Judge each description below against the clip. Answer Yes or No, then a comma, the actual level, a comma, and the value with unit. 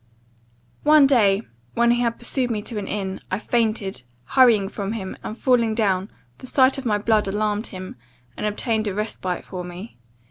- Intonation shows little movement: No, average, 3.3 semitones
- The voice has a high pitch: Yes, high, 215 Hz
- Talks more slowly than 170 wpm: No, average, 180 wpm